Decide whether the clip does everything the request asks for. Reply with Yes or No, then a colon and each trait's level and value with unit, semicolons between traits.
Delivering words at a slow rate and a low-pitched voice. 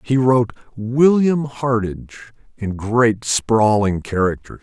Yes: slow, 105 wpm; low, 115 Hz